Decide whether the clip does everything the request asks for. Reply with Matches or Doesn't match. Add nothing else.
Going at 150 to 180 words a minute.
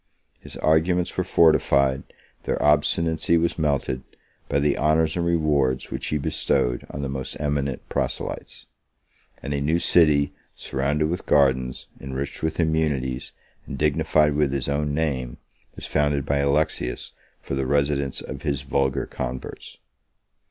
Doesn't match